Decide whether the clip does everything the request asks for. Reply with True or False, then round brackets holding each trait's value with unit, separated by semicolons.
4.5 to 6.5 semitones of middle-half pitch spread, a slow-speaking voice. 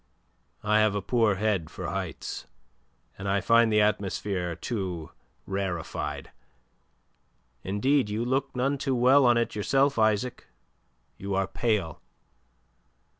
False (3.9 semitones; 125 wpm)